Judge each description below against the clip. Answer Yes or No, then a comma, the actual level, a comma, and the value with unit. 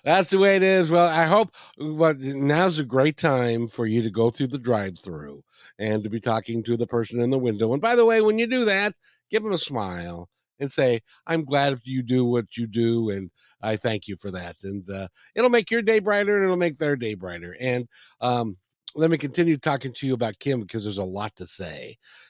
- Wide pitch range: Yes, wide, 6.9 semitones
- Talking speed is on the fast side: Yes, fast, 235 wpm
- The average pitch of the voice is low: Yes, low, 125 Hz